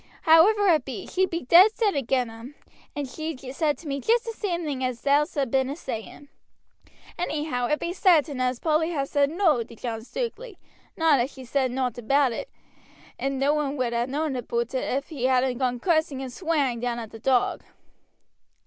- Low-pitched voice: No, very high, 280 Hz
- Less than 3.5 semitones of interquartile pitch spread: No, average, 4.3 semitones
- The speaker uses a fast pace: No, average, 195 wpm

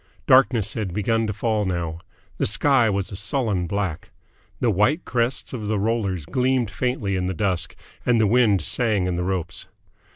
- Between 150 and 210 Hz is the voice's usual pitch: No, low, 105 Hz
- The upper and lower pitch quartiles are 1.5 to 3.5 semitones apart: No, average, 4.0 semitones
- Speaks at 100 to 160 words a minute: No, average, 175 wpm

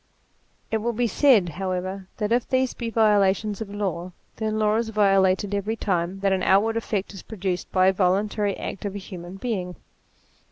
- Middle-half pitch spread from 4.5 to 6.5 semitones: No, average, 2.7 semitones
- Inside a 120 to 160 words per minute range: No, average, 190 wpm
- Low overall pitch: No, high, 200 Hz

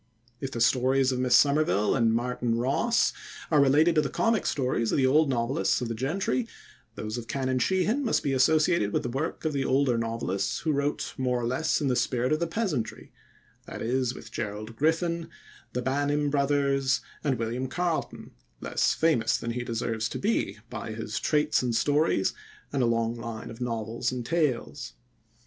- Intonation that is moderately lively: Yes, average, 4.1 semitones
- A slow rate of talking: No, average, 185 wpm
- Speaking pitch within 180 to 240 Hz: No, low, 130 Hz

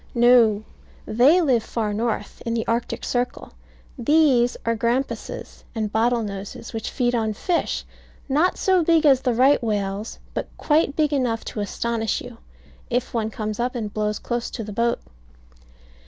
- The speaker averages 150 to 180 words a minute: Yes, average, 160 wpm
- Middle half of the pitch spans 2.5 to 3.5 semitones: Yes, average, 2.8 semitones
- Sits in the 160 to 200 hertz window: No, high, 235 Hz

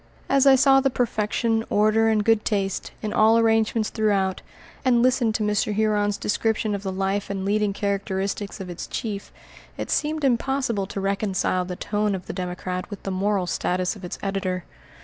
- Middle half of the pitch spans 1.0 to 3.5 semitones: Yes, narrow, 2.4 semitones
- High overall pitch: Yes, high, 210 Hz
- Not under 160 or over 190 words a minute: Yes, average, 180 wpm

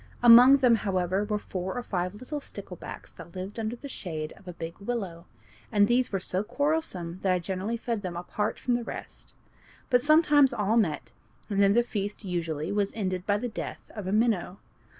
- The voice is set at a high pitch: Yes, high, 205 Hz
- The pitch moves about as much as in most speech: Yes, average, 4.6 semitones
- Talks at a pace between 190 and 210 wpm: Yes, average, 195 wpm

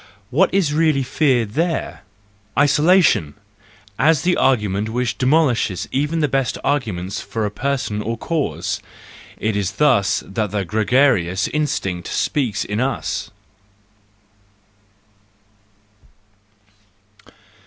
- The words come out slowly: Yes, slow, 100 wpm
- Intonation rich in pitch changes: Yes, wide, 6.3 semitones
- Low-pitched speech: Yes, low, 125 Hz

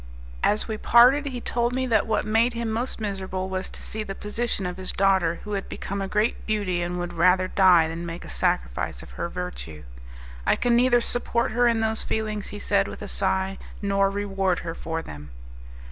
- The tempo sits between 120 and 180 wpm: No, fast, 205 wpm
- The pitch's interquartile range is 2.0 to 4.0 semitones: Yes, average, 3.6 semitones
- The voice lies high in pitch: Yes, high, 200 Hz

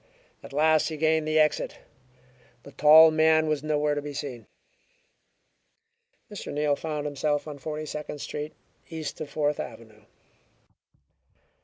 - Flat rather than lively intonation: Yes, narrow, 1.3 semitones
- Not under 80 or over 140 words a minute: Yes, slow, 135 wpm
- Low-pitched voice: No, medium, 150 Hz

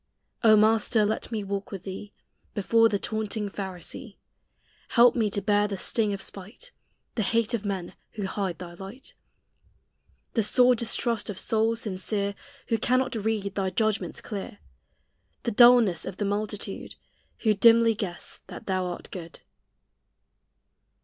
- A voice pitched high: Yes, high, 210 Hz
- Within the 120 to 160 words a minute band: Yes, average, 145 wpm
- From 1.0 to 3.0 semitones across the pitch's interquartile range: Yes, narrow, 2.5 semitones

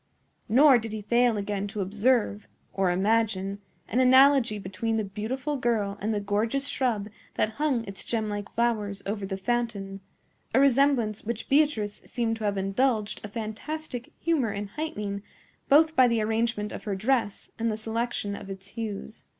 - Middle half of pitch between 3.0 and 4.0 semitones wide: Yes, average, 3.3 semitones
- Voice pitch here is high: Yes, high, 220 Hz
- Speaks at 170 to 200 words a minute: No, average, 160 wpm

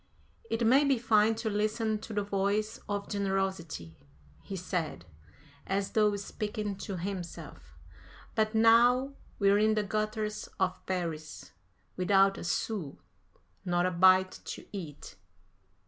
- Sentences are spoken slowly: Yes, slow, 130 wpm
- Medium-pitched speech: No, high, 200 Hz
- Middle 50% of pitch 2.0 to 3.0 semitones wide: Yes, narrow, 2.6 semitones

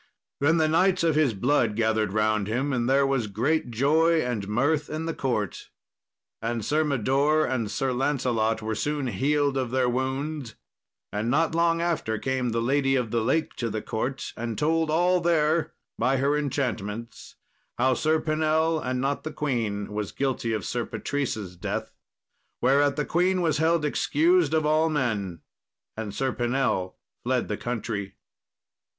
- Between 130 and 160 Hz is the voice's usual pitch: Yes, low, 135 Hz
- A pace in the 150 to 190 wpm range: Yes, average, 165 wpm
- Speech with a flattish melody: No, average, 5.2 semitones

